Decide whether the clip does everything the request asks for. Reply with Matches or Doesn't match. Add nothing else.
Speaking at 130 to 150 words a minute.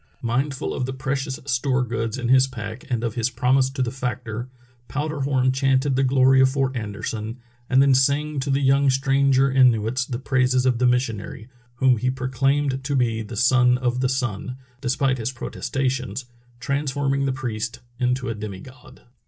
Doesn't match